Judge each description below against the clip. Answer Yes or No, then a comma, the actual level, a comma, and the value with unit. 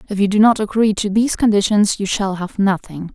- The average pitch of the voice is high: Yes, high, 200 Hz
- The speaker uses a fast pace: Yes, fast, 230 wpm